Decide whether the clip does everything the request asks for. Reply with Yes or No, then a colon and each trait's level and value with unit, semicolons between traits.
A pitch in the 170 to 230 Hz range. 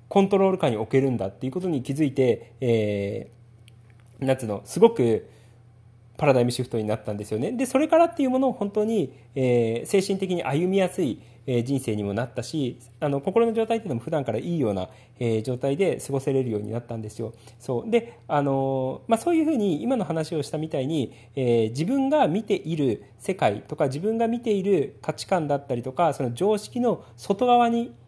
No: low, 135 Hz